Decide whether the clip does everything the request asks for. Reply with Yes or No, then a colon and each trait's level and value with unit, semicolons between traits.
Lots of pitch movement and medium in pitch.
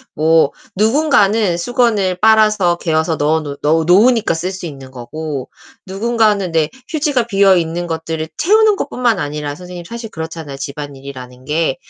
Yes: wide, 6.0 semitones; medium, 175 Hz